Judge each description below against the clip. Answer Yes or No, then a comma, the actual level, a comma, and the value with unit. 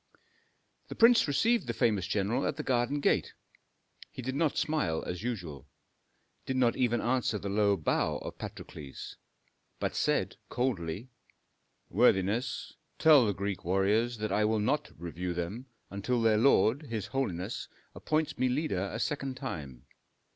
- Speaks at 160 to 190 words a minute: No, average, 145 wpm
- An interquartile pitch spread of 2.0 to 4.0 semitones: No, wide, 5.4 semitones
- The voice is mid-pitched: No, low, 115 Hz